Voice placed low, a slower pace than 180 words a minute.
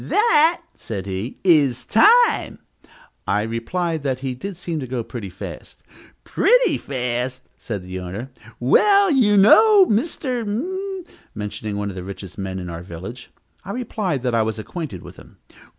Yes: low, 130 Hz; average, 165 wpm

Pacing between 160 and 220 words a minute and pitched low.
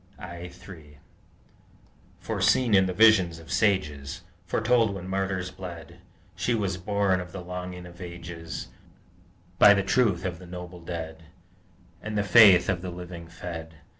No: average, 145 wpm; very low, 90 Hz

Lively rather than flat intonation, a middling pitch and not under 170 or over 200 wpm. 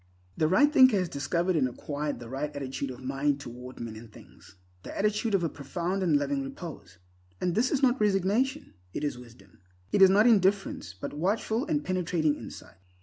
Yes: wide, 6.8 semitones; medium, 155 Hz; average, 185 wpm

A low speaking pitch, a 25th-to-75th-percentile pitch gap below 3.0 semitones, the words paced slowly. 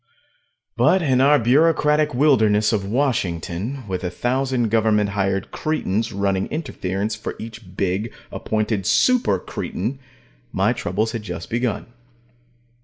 No: low, 110 Hz; average, 5.0 semitones; slow, 120 wpm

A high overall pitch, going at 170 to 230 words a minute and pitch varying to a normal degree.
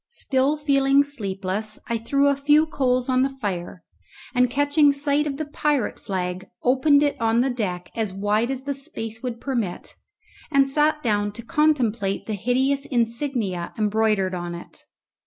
No: very high, 250 Hz; average, 160 wpm; average, 5.0 semitones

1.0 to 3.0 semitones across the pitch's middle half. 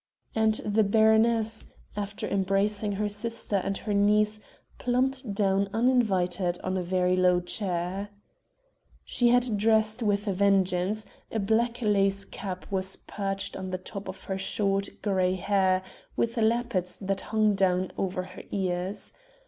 Yes: narrow, 2.5 semitones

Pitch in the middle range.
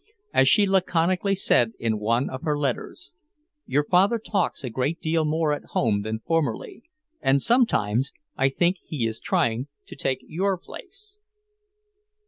Yes: medium, 150 Hz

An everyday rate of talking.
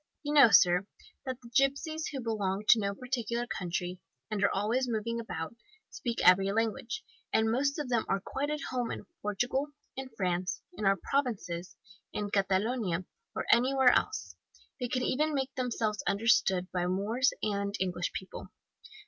Yes: average, 160 wpm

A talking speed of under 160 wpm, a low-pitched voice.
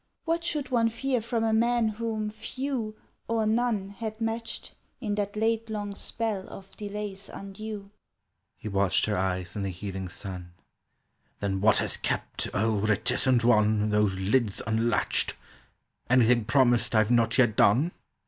No: average, 150 wpm; high, 195 Hz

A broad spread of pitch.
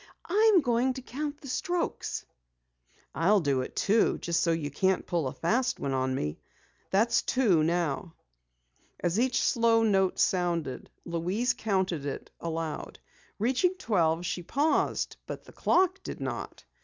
Yes: wide, 7.2 semitones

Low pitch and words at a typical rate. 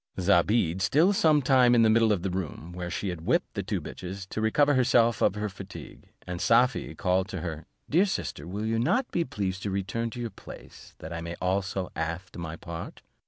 No: very low, 95 Hz; fast, 215 wpm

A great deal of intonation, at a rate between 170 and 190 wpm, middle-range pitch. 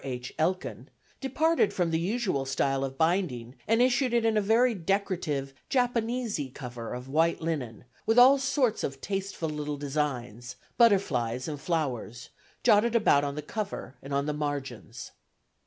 No: wide, 8.4 semitones; average, 155 wpm; medium, 160 Hz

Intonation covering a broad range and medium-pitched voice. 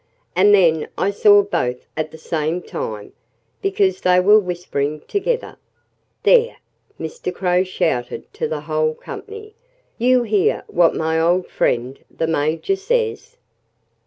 Yes: wide, 8.5 semitones; medium, 180 Hz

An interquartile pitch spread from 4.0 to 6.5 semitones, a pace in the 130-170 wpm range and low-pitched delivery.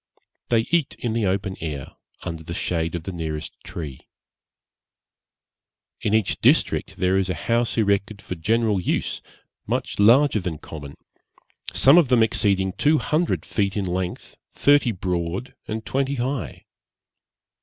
Yes: average, 5.1 semitones; average, 145 wpm; low, 100 Hz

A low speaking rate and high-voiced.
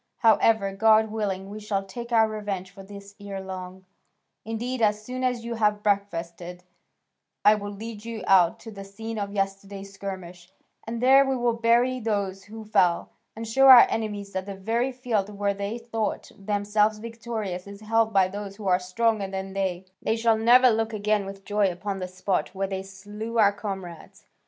No: average, 185 wpm; high, 205 Hz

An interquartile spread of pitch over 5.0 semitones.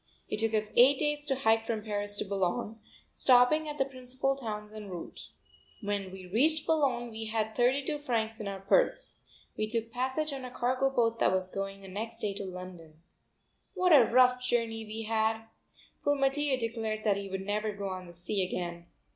No: average, 4.2 semitones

